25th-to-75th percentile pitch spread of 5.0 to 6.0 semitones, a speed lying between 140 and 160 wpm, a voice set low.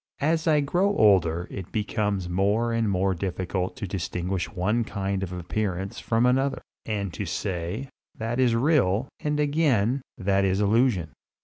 No: average, 4.4 semitones; average, 150 wpm; low, 100 Hz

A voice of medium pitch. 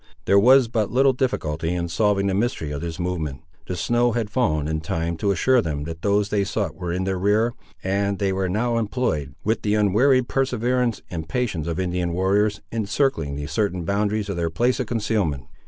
No: low, 100 Hz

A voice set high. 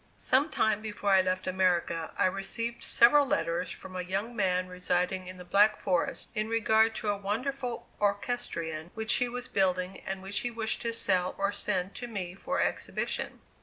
Yes: high, 200 Hz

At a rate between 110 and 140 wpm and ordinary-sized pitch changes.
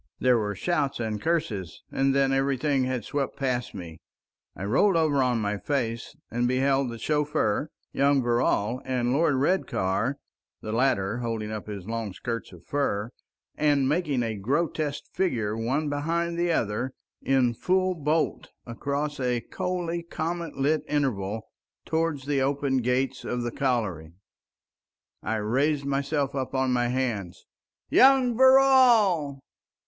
Yes: slow, 135 wpm; average, 4.4 semitones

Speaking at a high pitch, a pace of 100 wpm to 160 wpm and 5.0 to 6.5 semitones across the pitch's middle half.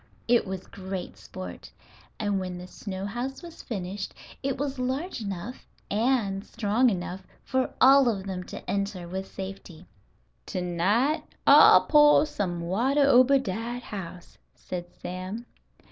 Yes: high, 200 Hz; average, 140 wpm; wide, 5.6 semitones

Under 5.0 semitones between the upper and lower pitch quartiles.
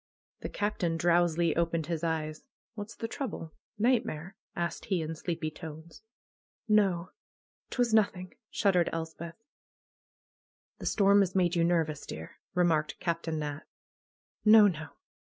Yes: average, 3.6 semitones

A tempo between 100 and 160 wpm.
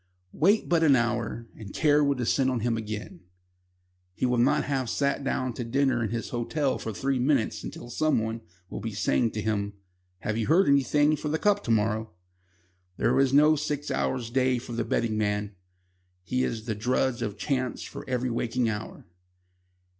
No: average, 185 wpm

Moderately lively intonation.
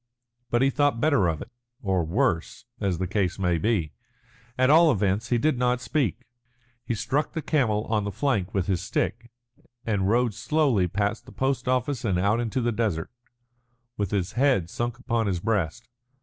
Yes: average, 4.9 semitones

